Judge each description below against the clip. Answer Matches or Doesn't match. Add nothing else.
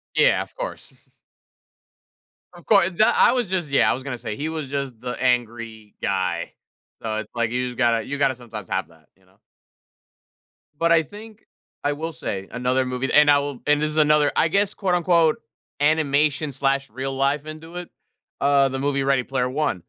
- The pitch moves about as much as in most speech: Matches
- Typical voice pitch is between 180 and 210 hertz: Doesn't match